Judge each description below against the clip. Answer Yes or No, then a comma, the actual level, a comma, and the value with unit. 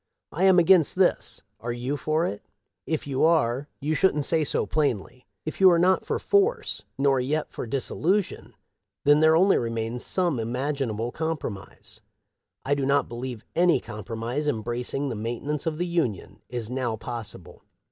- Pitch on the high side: No, medium, 140 Hz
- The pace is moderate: Yes, average, 160 wpm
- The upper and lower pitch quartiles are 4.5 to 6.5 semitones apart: Yes, average, 5.2 semitones